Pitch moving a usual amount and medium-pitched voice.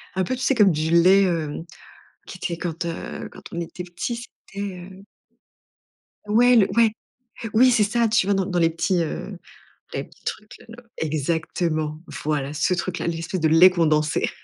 Yes: average, 3.6 semitones; medium, 175 Hz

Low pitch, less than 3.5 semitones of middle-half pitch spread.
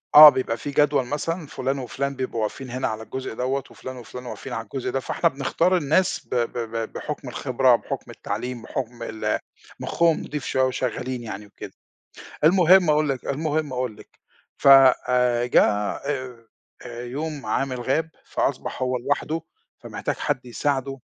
Yes: low, 130 Hz; average, 3.1 semitones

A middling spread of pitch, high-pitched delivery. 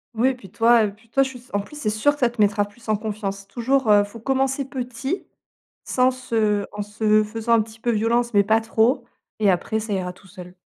Yes: average, 3.2 semitones; high, 225 Hz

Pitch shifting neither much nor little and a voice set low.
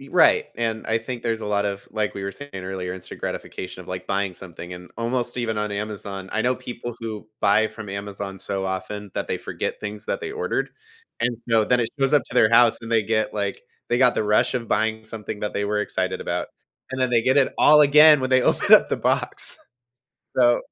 Yes: average, 3.2 semitones; low, 110 Hz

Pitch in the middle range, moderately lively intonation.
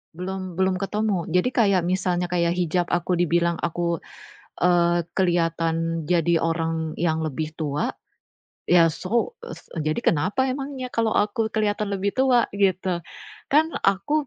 Yes: medium, 180 Hz; average, 3.6 semitones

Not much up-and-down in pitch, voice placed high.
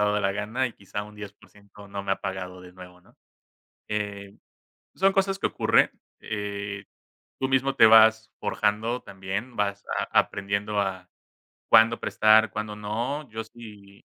No: narrow, 2.0 semitones; low, 105 Hz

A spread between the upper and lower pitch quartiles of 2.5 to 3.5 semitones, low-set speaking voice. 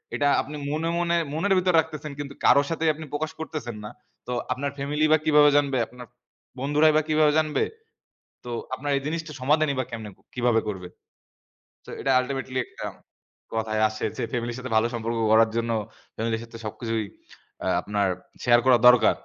No: average, 4.8 semitones; low, 130 Hz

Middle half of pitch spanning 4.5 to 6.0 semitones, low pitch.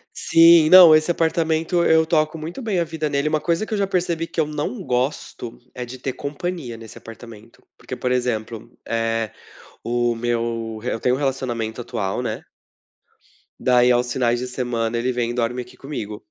Yes: average, 5.3 semitones; low, 125 Hz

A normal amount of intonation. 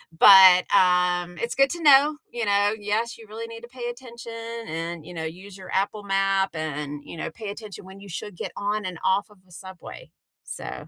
Yes: average, 4.1 semitones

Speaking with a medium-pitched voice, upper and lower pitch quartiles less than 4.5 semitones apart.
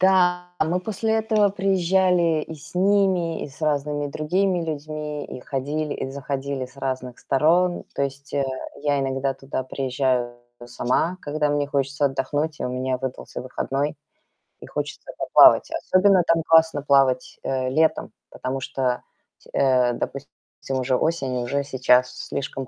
Yes: medium, 145 Hz; average, 4.0 semitones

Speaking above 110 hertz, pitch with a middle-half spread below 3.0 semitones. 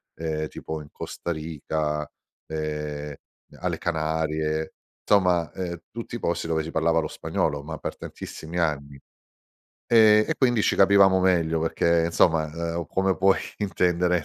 No: very low, 80 Hz; narrow, 2.6 semitones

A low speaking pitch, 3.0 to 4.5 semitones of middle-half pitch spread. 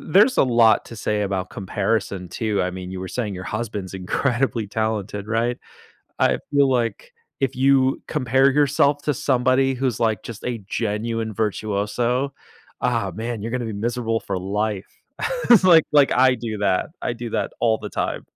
Yes: low, 115 Hz; average, 3.9 semitones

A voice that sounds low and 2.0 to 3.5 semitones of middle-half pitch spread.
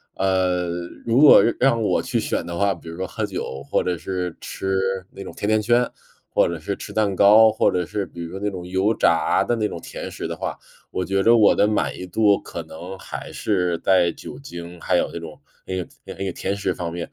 Yes: very low, 95 Hz; average, 3.1 semitones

